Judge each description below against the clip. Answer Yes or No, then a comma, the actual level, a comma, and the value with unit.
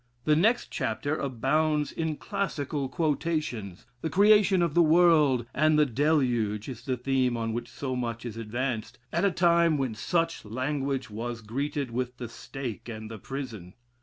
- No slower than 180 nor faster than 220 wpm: No, average, 165 wpm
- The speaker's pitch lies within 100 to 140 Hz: Yes, low, 135 Hz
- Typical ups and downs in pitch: Yes, average, 4.9 semitones